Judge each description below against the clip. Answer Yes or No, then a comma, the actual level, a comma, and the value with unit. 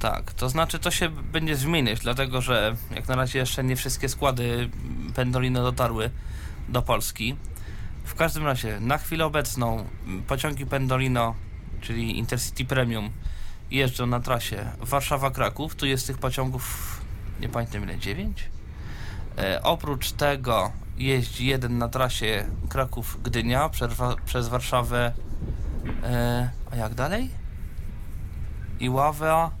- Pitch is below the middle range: Yes, low, 120 Hz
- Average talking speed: Yes, average, 120 wpm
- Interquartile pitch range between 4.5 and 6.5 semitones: No, average, 4.0 semitones